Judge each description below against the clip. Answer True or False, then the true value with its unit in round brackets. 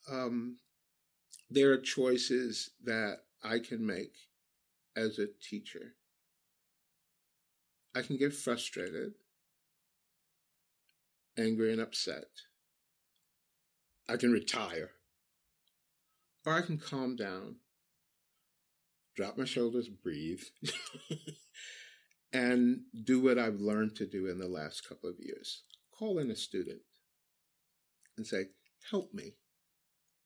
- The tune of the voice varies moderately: False (6.1 semitones)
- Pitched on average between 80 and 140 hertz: True (135 Hz)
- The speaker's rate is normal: False (100 wpm)